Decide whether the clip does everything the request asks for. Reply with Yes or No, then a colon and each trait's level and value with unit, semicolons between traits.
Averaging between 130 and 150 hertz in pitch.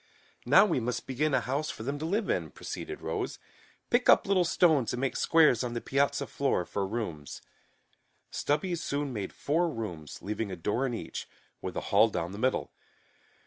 Yes: low, 135 Hz